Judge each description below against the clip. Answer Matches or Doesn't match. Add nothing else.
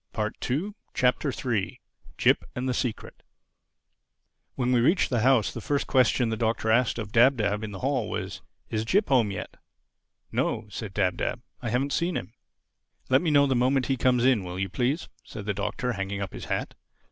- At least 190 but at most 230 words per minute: Matches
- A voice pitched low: Matches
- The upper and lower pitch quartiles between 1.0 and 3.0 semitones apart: Doesn't match